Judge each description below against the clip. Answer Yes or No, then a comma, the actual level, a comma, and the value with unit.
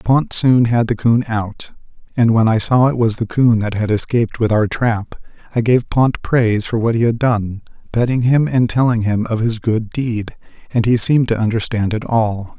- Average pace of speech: No, fast, 215 wpm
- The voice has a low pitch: Yes, low, 115 Hz